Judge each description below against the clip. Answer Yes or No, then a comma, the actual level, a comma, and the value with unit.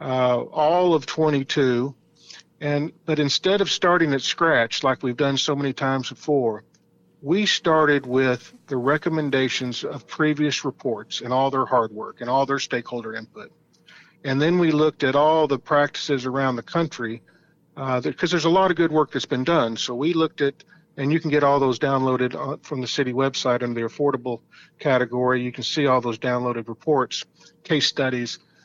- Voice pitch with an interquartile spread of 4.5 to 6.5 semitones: No, average, 3.4 semitones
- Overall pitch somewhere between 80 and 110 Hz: No, medium, 140 Hz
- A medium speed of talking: Yes, average, 180 wpm